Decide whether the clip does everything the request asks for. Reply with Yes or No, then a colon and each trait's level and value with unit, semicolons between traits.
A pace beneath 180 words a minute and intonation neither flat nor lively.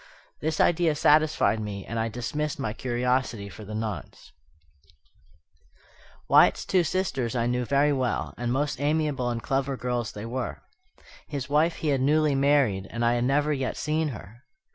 Yes: average, 165 wpm; average, 4.0 semitones